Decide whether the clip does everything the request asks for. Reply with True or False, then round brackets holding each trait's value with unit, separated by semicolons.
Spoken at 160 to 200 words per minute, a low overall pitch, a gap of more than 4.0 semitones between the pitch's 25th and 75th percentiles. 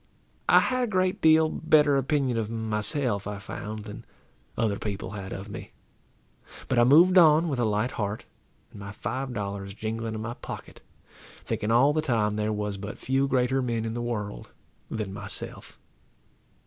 True (175 wpm; 115 Hz; 4.7 semitones)